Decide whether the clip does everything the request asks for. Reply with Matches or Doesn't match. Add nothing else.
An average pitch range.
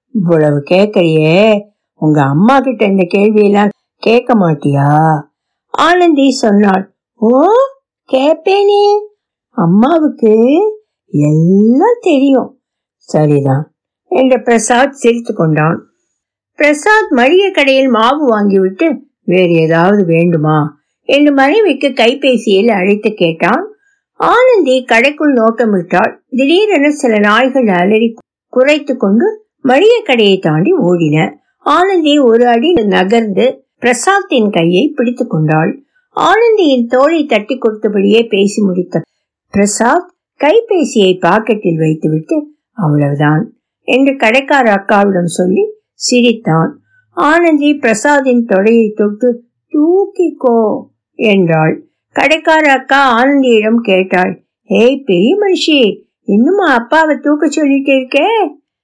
Doesn't match